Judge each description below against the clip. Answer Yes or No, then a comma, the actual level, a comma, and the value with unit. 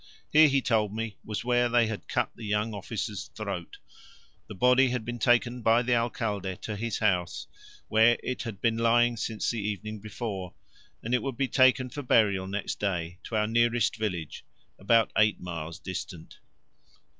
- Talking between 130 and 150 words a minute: No, average, 175 wpm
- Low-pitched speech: Yes, low, 110 Hz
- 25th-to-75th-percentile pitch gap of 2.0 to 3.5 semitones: Yes, average, 2.9 semitones